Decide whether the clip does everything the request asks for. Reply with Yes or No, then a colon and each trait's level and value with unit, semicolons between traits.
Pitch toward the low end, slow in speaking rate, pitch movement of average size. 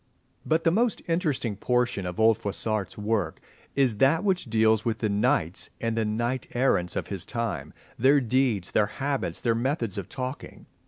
No: low, 115 Hz; average, 170 wpm; average, 4.2 semitones